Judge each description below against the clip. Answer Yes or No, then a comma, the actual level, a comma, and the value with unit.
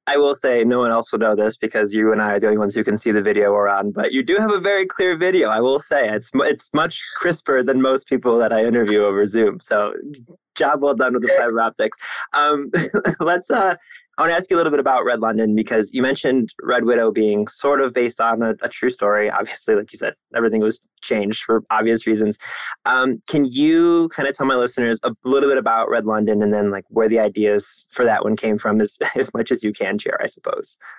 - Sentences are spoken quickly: Yes, fast, 245 wpm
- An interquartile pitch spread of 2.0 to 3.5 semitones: No, average, 4.3 semitones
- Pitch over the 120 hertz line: No, low, 115 Hz